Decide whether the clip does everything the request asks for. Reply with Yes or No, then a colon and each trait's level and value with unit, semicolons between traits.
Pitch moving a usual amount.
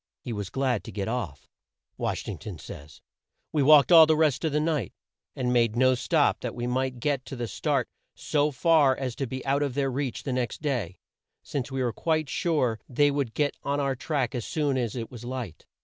Yes: average, 3.2 semitones